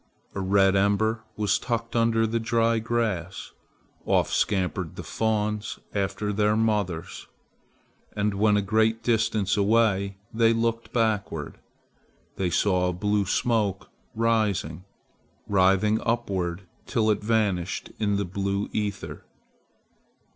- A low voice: Yes, low, 105 Hz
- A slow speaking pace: Yes, slow, 120 wpm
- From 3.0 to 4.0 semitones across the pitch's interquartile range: No, narrow, 2.4 semitones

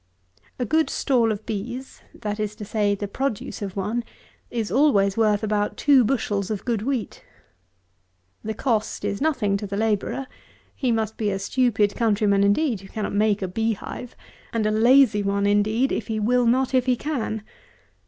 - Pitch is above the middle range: Yes, high, 220 Hz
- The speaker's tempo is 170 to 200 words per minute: Yes, average, 185 wpm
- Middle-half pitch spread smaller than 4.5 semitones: Yes, average, 3.2 semitones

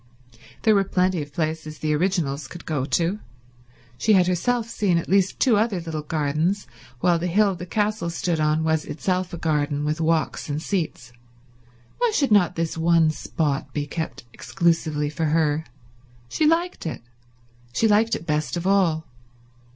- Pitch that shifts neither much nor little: Yes, average, 3.8 semitones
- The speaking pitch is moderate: Yes, medium, 165 Hz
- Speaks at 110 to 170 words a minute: Yes, average, 165 wpm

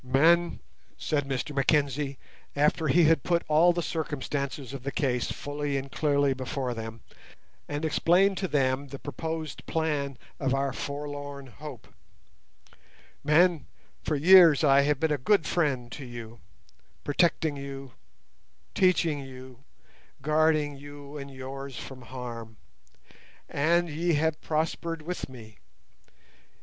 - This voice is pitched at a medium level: Yes, medium, 145 Hz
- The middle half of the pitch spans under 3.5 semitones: Yes, average, 2.9 semitones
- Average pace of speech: No, slow, 125 wpm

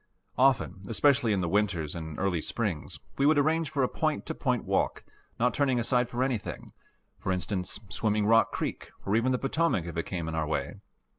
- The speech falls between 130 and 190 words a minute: No, average, 200 wpm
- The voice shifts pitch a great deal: Yes, wide, 6.5 semitones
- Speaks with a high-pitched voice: No, low, 110 Hz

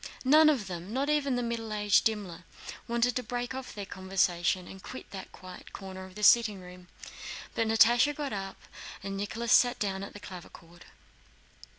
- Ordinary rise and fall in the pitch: Yes, average, 4.5 semitones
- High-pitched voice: Yes, high, 210 Hz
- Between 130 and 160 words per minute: No, average, 175 wpm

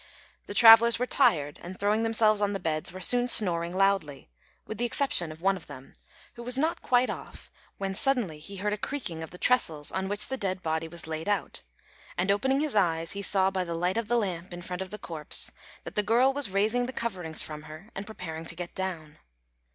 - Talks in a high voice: Yes, high, 195 Hz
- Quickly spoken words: Yes, fast, 225 wpm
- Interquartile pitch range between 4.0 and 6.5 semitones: Yes, average, 5.2 semitones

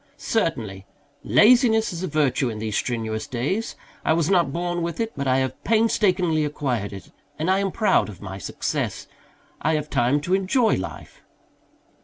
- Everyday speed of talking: Yes, average, 170 wpm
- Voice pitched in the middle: Yes, medium, 155 Hz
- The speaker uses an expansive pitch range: Yes, wide, 8.0 semitones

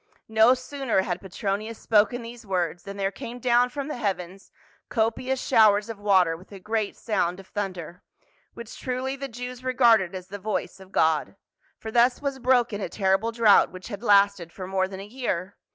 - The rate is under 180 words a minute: No, average, 185 wpm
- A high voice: Yes, high, 210 Hz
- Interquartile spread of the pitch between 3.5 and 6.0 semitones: Yes, average, 4.0 semitones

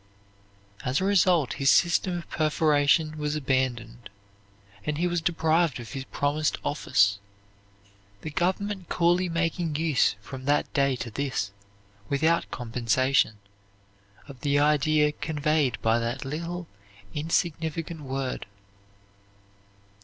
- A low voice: No, medium, 150 Hz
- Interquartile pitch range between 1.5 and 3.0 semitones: No, average, 4.0 semitones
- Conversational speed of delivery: No, slow, 115 wpm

